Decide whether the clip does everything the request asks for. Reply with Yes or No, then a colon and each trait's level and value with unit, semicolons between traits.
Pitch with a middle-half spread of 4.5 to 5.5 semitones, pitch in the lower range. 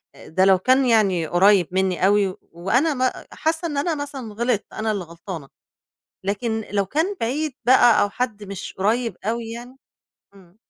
No: average, 5.0 semitones; high, 215 Hz